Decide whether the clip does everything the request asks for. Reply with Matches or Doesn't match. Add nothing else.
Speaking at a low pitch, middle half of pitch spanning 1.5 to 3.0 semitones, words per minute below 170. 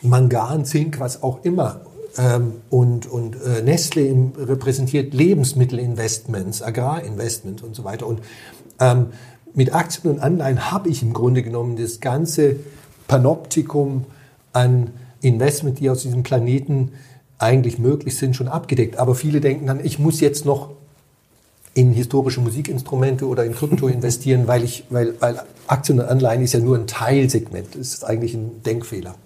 Matches